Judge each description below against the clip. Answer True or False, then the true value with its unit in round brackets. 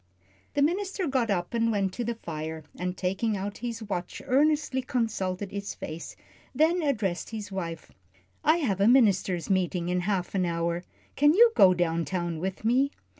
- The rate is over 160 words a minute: True (175 wpm)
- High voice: True (200 Hz)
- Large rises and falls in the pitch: True (5.9 semitones)